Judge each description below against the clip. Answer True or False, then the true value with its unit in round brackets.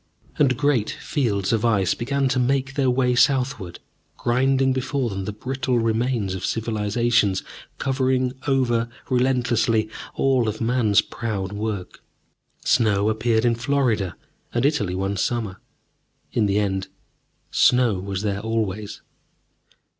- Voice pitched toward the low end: True (115 Hz)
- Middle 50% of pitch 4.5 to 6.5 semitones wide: False (3.8 semitones)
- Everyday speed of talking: False (125 wpm)